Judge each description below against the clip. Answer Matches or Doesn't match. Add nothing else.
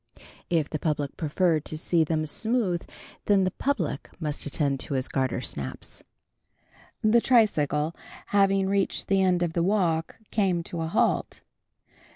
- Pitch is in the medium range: Matches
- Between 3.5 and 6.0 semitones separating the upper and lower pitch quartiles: Matches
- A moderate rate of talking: Matches